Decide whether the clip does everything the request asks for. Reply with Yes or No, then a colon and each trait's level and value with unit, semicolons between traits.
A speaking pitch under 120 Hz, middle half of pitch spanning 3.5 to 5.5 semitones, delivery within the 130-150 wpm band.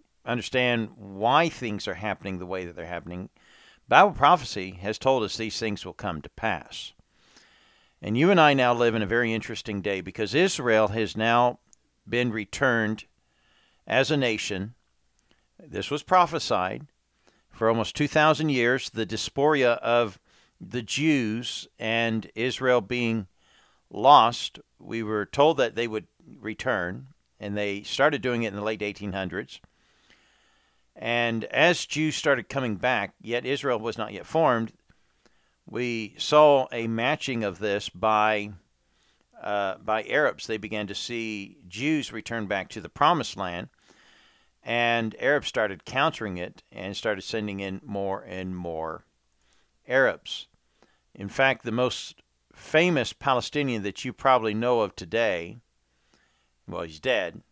Yes: low, 110 Hz; average, 3.8 semitones; average, 140 wpm